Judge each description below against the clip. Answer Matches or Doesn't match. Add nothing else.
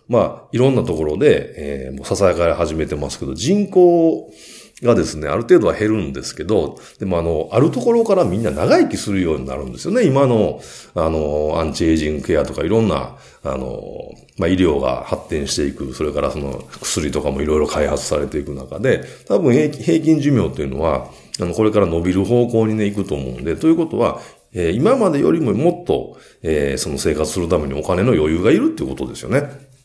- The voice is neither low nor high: Doesn't match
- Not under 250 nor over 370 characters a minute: Doesn't match